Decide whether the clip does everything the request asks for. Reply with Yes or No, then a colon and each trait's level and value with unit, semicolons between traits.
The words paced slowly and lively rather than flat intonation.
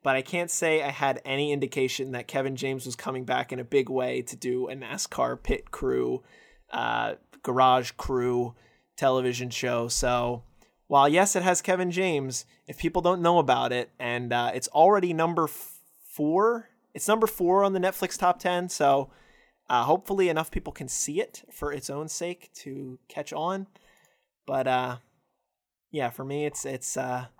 No: average, 175 wpm; wide, 5.7 semitones